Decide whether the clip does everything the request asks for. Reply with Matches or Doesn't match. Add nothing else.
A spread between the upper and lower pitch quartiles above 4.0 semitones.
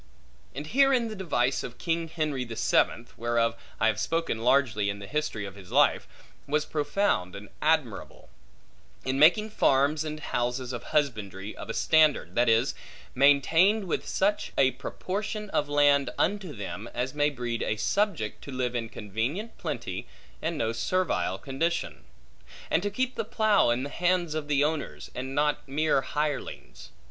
Matches